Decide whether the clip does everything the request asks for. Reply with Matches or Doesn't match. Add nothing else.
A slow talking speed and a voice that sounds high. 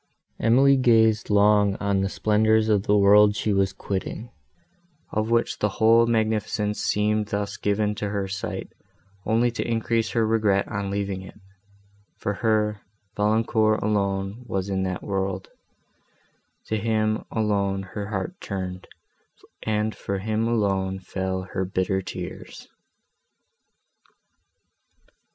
Doesn't match